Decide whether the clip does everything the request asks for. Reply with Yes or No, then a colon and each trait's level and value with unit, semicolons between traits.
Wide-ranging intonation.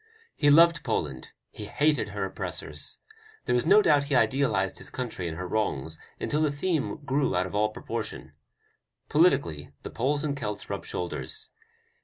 Yes: wide, 8.0 semitones